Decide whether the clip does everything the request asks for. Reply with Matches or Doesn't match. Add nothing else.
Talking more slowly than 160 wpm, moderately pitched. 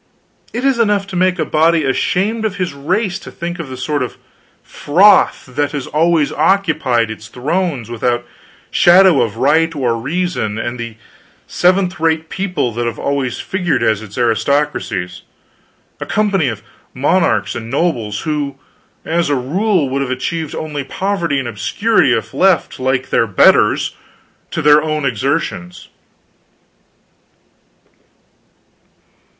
Matches